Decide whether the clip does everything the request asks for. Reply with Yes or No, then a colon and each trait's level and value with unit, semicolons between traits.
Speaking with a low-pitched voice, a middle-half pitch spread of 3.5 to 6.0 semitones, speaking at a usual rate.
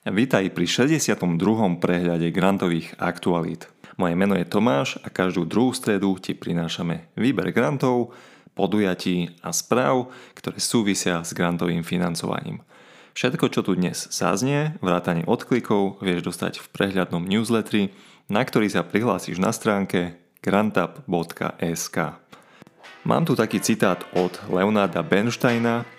Yes: very low, 95 Hz; average, 4.5 semitones; average, 120 wpm